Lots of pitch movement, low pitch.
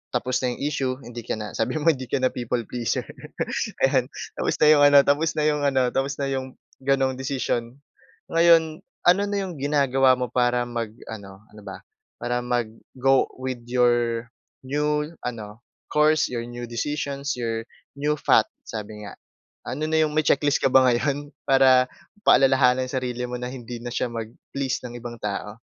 No: average, 3.0 semitones; low, 130 Hz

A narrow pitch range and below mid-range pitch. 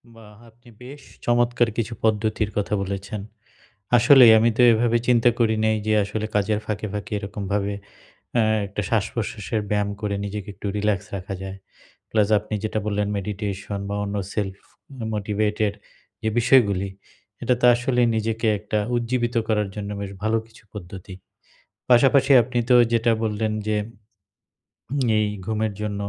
Yes: narrow, 2.3 semitones; low, 105 Hz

